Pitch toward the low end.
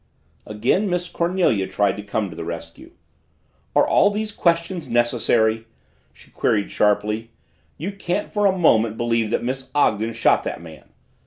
Yes: low, 115 Hz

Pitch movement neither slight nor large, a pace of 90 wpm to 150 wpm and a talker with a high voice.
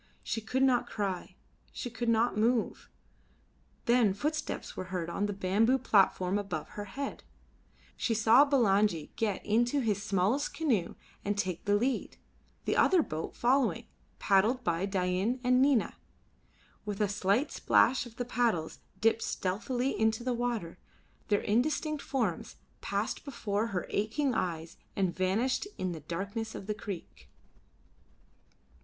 Yes: average, 4.2 semitones; average, 140 wpm; high, 220 Hz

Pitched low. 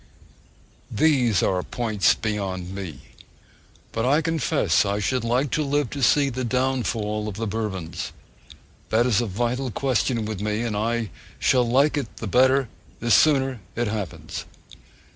Yes: low, 115 Hz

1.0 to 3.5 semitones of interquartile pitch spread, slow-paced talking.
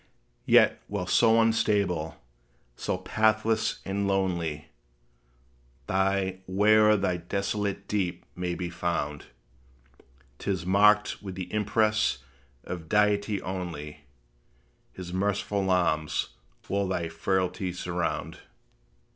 Yes: average, 2.7 semitones; slow, 105 wpm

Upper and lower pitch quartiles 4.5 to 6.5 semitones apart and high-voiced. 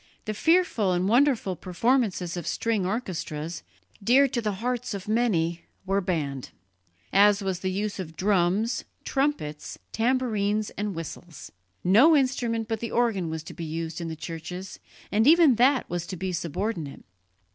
Yes: average, 5.1 semitones; high, 200 Hz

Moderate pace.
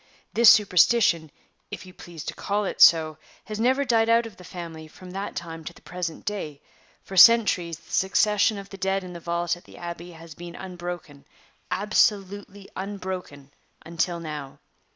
Yes: average, 170 wpm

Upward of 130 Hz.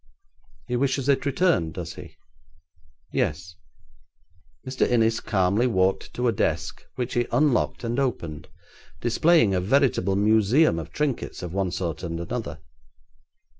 No: low, 115 Hz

